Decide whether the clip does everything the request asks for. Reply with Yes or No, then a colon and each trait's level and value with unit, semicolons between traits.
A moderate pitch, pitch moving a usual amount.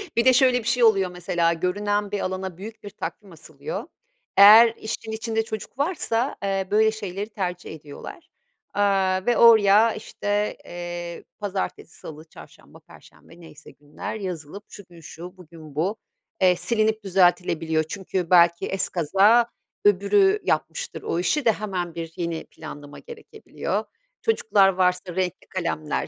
No: high, 195 Hz; average, 4.0 semitones